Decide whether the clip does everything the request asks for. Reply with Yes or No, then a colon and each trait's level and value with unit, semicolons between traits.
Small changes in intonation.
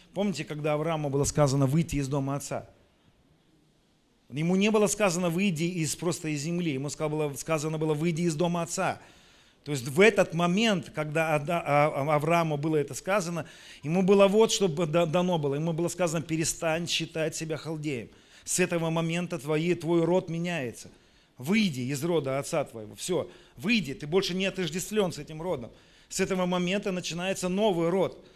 No: average, 3.2 semitones